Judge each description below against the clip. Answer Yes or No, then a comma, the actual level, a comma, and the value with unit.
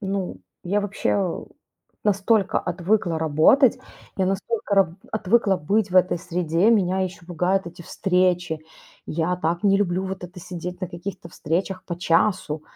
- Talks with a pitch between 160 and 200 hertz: Yes, medium, 185 Hz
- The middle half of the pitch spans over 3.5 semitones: No, narrow, 2.4 semitones